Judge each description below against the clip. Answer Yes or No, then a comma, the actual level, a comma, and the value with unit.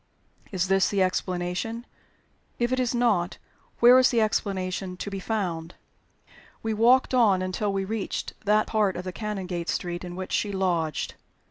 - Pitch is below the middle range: No, high, 195 Hz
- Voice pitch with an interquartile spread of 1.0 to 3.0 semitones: No, average, 3.4 semitones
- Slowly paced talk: No, average, 160 wpm